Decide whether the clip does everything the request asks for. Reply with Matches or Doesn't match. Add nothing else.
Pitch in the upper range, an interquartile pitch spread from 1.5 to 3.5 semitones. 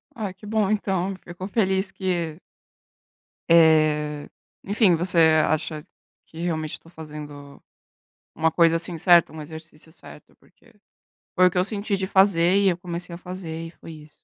Doesn't match